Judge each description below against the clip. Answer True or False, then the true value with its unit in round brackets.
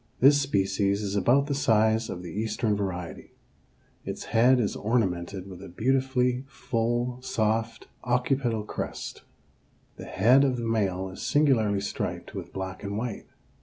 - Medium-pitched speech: False (110 Hz)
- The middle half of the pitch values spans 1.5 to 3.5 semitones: False (3.9 semitones)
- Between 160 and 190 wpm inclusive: False (145 wpm)